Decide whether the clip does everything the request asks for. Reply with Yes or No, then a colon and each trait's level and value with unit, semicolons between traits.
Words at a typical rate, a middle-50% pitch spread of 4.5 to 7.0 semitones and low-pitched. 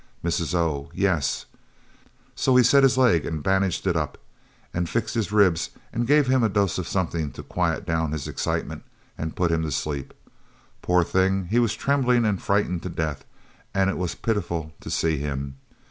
Yes: average, 185 wpm; average, 4.8 semitones; very low, 90 Hz